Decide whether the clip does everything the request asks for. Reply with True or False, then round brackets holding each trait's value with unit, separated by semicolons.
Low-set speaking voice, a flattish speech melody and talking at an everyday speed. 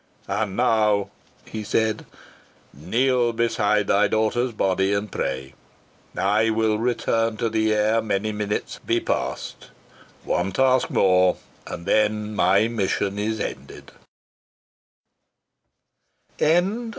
False (105 Hz; 2.1 semitones; 105 wpm)